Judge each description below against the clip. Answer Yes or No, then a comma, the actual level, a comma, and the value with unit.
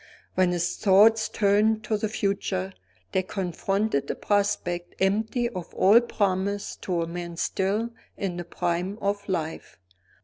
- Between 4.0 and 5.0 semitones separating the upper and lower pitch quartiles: No, average, 3.1 semitones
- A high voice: Yes, high, 195 Hz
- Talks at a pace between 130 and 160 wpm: Yes, average, 140 wpm